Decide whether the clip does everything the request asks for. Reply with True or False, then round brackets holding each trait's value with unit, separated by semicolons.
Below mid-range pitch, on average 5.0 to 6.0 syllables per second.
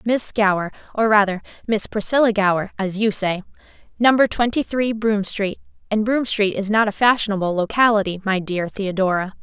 False (210 Hz; 5.5 syllables/s)